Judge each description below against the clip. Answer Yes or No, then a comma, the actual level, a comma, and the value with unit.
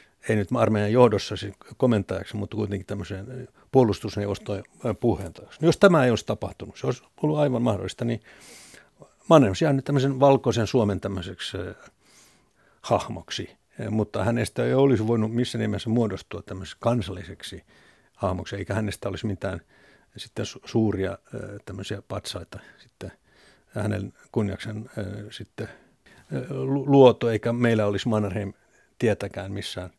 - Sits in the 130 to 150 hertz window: No, low, 105 Hz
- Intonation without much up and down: No, average, 3.2 semitones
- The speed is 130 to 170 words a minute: No, average, 120 wpm